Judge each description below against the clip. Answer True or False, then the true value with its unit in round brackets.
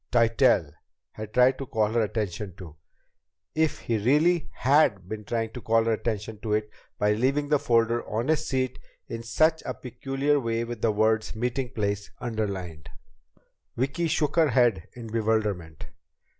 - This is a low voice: True (115 Hz)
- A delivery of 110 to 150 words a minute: False (160 wpm)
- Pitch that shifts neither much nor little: True (3.6 semitones)